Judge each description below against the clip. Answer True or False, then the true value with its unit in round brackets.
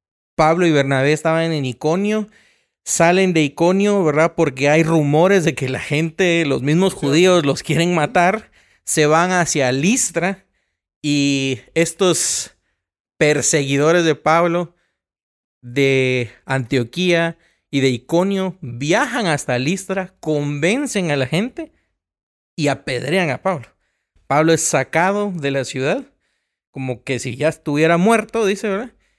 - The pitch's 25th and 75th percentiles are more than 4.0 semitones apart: True (4.4 semitones)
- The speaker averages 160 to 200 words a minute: False (125 wpm)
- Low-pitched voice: False (160 Hz)